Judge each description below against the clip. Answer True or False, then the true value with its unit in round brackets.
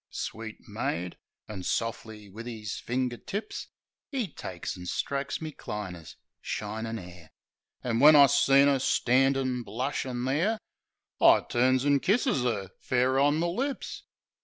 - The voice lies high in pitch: False (125 Hz)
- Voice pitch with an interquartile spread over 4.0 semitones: True (4.5 semitones)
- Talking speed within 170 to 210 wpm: False (135 wpm)